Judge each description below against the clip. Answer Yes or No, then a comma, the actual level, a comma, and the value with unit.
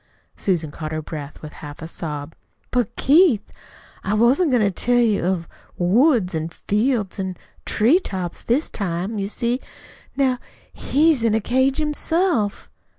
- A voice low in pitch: No, high, 215 Hz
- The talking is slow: No, average, 155 wpm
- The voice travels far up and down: Yes, wide, 6.7 semitones